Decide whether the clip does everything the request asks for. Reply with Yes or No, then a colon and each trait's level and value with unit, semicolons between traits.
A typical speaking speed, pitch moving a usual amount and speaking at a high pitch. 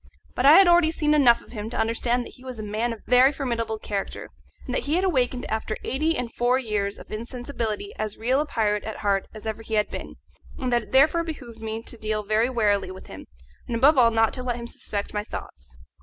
No: fast, 245 wpm; average, 3.2 semitones; high, 235 Hz